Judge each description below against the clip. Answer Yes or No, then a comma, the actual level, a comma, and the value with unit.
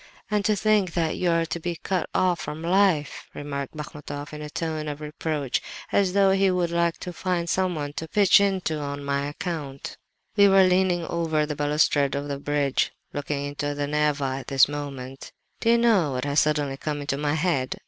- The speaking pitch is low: No, medium, 150 Hz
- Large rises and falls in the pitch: No, average, 3.8 semitones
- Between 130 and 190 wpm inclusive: No, average, 200 wpm